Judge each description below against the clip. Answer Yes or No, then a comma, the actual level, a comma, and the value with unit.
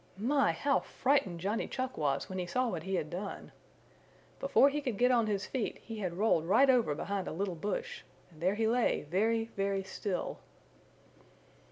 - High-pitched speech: Yes, high, 205 Hz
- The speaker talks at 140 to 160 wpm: No, average, 185 wpm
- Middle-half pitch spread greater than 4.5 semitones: Yes, average, 5.2 semitones